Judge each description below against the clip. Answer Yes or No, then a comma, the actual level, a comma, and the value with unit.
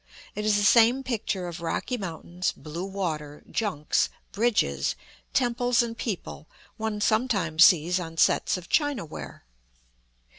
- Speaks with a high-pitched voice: Yes, high, 195 Hz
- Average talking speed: No, slow, 125 wpm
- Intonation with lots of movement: Yes, wide, 5.7 semitones